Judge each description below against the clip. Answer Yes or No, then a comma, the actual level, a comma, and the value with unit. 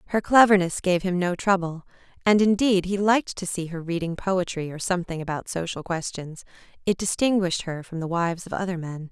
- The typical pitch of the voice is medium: Yes, medium, 180 Hz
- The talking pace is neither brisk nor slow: Yes, average, 190 wpm